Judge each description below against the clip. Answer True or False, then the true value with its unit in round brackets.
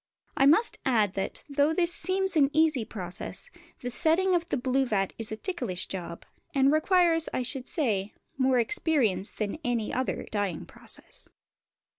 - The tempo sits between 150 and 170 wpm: True (160 wpm)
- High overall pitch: True (265 Hz)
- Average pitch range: False (7.0 semitones)